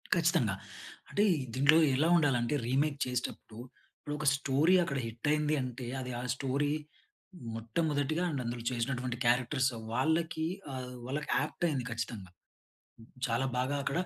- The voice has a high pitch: No, low, 135 Hz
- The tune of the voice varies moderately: Yes, average, 3.6 semitones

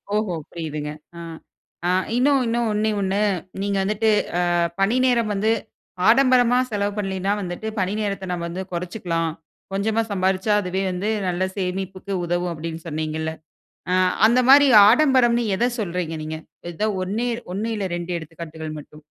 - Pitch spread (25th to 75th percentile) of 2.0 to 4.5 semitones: Yes, average, 4.2 semitones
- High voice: Yes, high, 195 Hz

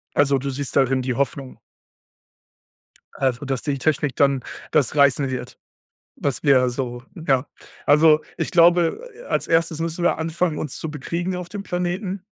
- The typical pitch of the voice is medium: Yes, medium, 145 Hz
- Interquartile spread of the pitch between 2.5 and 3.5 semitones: No, average, 4.0 semitones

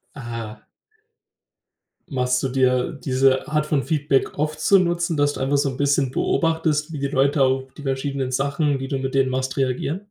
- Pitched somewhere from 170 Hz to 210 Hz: No, low, 135 Hz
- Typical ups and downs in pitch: No, narrow, 2.2 semitones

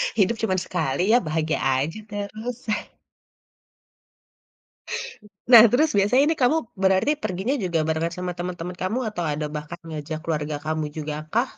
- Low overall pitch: No, medium, 180 Hz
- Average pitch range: No, wide, 5.7 semitones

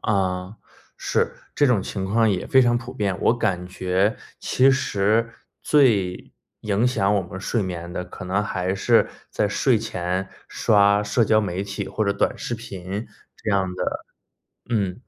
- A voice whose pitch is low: Yes, low, 100 Hz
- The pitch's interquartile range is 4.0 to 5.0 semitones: No, average, 3.4 semitones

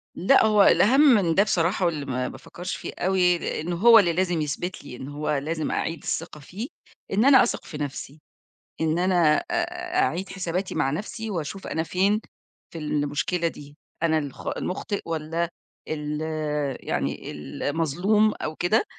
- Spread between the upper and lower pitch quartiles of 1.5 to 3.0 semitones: No, average, 4.3 semitones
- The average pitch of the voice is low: No, medium, 170 Hz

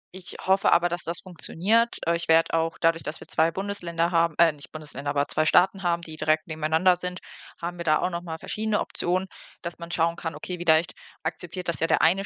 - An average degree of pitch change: No, narrow, 1.9 semitones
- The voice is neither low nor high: Yes, medium, 170 Hz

